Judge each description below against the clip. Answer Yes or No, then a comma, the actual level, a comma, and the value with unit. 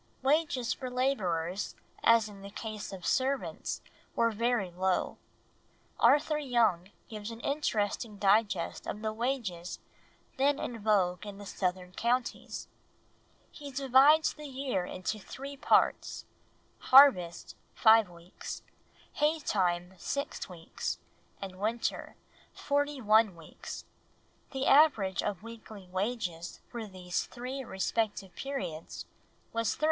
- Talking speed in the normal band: No, slow, 120 wpm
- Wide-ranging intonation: Yes, wide, 5.7 semitones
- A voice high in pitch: Yes, high, 220 Hz